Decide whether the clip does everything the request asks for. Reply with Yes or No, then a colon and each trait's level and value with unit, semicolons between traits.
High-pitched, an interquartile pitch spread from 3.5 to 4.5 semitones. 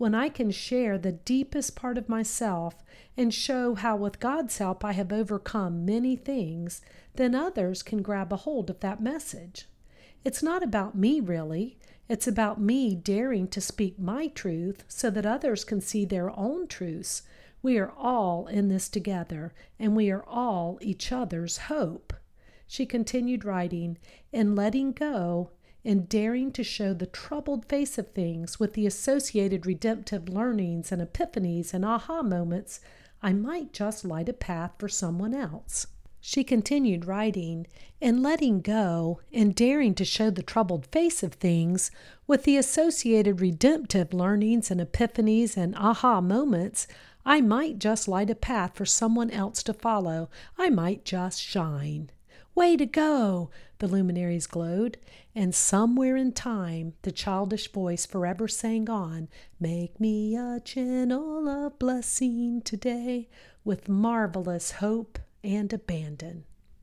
No: high, 215 Hz; average, 4.9 semitones